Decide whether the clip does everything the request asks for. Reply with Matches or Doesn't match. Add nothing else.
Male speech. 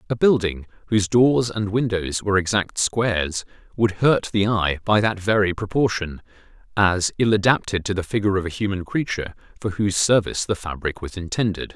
Matches